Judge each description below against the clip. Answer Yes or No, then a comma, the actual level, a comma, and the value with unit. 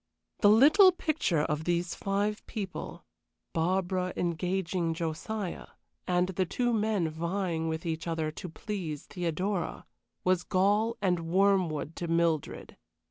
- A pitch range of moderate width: Yes, average, 3.4 semitones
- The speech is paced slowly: Yes, slow, 125 wpm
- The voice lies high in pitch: No, medium, 180 Hz